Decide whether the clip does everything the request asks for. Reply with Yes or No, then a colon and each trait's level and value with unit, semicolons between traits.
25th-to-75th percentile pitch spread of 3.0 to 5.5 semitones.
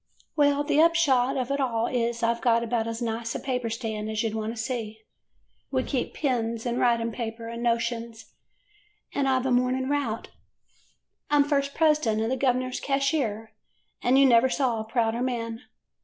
No: narrow, 2.6 semitones